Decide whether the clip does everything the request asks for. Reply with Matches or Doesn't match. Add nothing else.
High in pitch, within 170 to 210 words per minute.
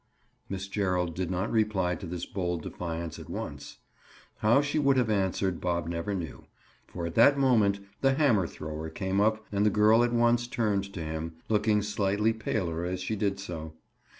Doesn't match